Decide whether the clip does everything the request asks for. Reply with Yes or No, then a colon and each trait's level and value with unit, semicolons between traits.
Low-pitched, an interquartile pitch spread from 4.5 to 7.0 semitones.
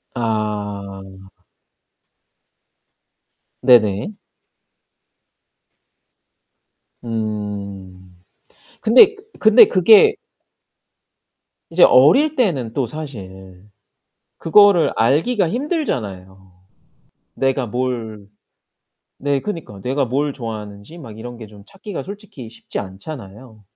No: low, 115 Hz; wide, 7.6 semitones